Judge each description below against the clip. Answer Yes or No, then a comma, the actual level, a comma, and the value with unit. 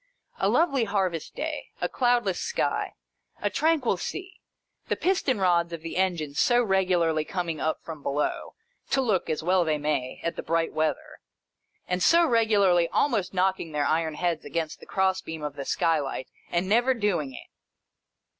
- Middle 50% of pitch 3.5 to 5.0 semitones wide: No, wide, 5.5 semitones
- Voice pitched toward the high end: No, medium, 180 Hz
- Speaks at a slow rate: No, average, 165 wpm